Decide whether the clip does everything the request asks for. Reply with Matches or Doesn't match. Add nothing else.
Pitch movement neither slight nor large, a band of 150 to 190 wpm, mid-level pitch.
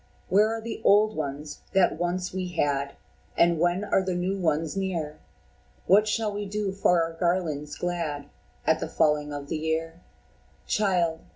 Matches